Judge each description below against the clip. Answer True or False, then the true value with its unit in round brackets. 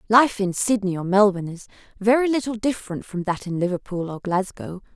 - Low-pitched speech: False (200 Hz)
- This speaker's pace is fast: False (180 wpm)